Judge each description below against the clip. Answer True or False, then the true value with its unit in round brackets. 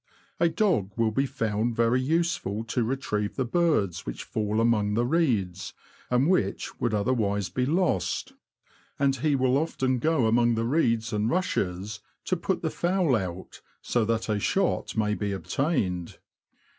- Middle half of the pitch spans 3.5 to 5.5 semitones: True (5.2 semitones)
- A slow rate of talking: False (160 wpm)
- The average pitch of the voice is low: True (115 Hz)